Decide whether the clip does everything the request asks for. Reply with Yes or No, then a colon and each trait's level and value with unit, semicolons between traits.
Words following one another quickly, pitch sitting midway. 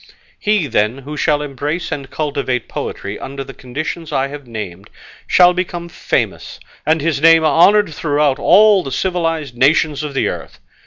No: average, 160 wpm; medium, 150 Hz